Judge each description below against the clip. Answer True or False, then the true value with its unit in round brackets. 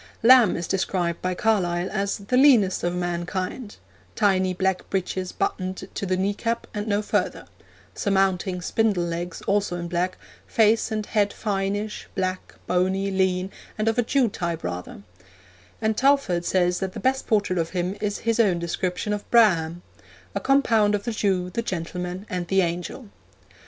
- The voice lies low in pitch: False (190 Hz)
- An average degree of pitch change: True (3.0 semitones)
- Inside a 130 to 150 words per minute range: False (165 wpm)